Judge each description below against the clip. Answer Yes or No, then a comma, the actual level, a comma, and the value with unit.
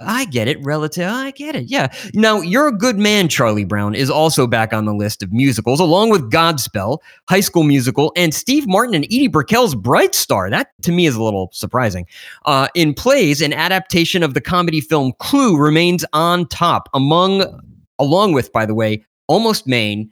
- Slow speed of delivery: No, average, 195 wpm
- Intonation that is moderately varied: No, wide, 7.0 semitones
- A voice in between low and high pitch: Yes, medium, 155 Hz